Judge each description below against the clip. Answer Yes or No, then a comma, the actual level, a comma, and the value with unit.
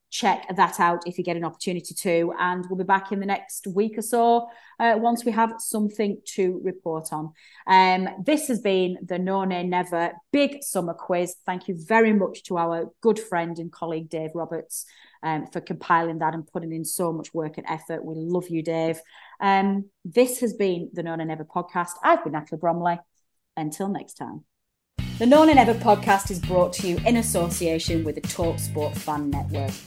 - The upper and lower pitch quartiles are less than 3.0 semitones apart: No, average, 3.5 semitones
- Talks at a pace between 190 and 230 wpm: Yes, average, 200 wpm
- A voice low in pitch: No, medium, 180 Hz